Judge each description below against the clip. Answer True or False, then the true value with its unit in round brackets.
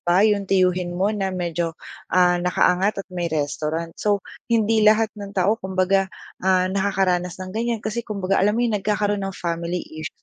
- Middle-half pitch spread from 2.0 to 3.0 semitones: True (2.6 semitones)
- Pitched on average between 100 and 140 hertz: False (190 Hz)